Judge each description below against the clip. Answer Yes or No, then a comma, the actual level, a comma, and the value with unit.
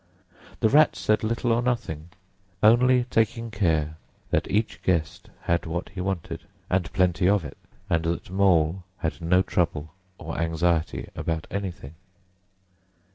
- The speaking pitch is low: Yes, very low, 90 Hz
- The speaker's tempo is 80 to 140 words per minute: Yes, slow, 135 wpm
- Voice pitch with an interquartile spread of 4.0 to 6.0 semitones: Yes, average, 4.7 semitones